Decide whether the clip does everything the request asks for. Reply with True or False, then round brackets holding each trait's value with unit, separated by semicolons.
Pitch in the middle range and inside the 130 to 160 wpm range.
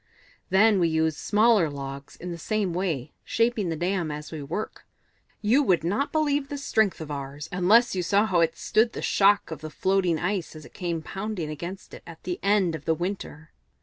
False (180 Hz; 205 wpm)